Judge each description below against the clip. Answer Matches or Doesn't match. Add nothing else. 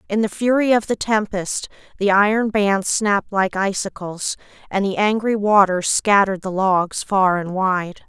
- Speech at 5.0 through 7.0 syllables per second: Doesn't match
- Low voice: Doesn't match